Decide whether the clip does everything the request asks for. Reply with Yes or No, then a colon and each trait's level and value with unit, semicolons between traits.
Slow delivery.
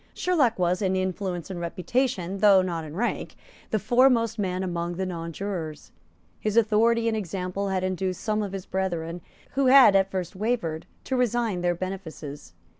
No: average, 165 wpm